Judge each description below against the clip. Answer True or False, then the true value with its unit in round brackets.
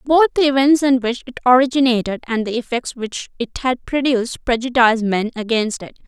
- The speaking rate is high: False (180 wpm)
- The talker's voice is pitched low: False (245 Hz)